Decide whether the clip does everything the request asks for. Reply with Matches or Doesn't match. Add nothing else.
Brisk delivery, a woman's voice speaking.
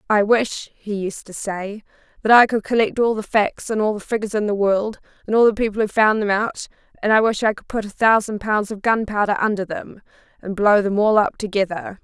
Matches